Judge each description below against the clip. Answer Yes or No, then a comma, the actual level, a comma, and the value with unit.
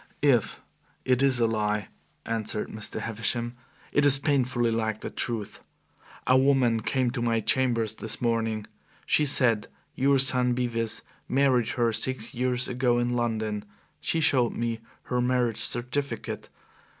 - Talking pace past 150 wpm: No, average, 140 wpm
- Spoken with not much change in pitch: Yes, narrow, 2.3 semitones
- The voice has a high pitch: No, low, 120 Hz